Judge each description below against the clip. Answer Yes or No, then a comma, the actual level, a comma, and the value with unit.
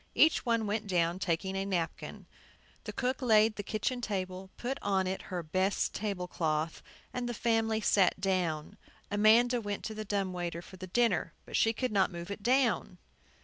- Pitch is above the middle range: Yes, high, 200 Hz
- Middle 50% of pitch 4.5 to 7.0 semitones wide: No, average, 3.5 semitones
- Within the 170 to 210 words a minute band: Yes, average, 185 wpm